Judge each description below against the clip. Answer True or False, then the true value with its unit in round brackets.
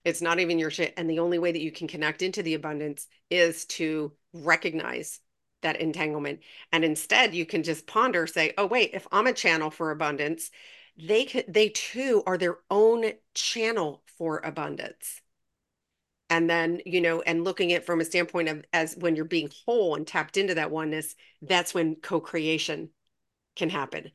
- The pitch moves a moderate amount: False (2.0 semitones)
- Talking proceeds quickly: False (180 wpm)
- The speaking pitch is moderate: True (165 Hz)